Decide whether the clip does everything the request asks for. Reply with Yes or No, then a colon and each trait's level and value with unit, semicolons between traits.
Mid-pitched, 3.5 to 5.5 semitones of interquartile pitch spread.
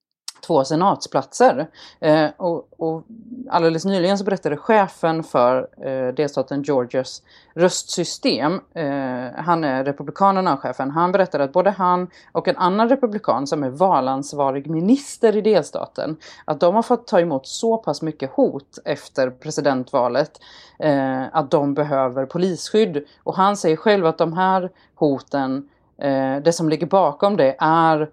Yes: medium, 160 Hz; average, 5.2 semitones